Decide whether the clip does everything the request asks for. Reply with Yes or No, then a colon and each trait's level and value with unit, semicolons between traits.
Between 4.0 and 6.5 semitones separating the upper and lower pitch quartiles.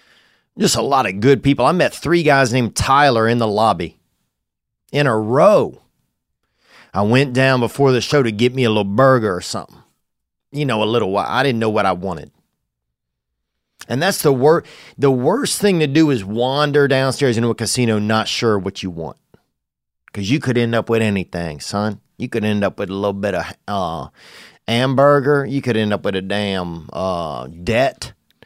Yes: average, 5.1 semitones